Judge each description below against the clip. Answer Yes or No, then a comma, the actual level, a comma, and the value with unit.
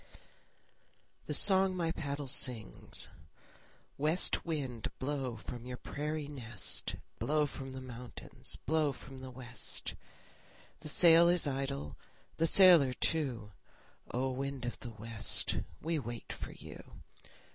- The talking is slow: Yes, slow, 125 wpm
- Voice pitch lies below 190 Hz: Yes, low, 135 Hz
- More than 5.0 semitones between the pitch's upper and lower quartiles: No, average, 4.0 semitones